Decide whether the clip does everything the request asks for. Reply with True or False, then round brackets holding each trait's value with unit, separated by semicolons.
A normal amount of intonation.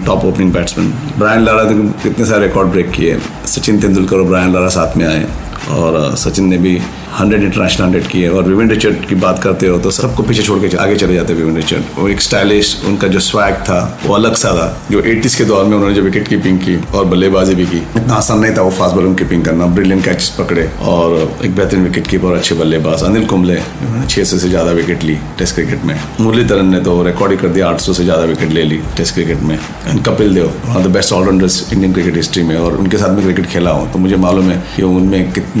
False (2.1 semitones)